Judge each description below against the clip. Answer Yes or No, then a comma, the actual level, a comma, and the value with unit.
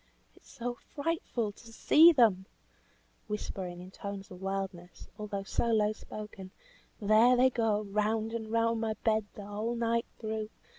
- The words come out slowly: No, average, 155 wpm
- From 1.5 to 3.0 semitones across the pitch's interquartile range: Yes, narrow, 2.4 semitones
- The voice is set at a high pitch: Yes, high, 215 Hz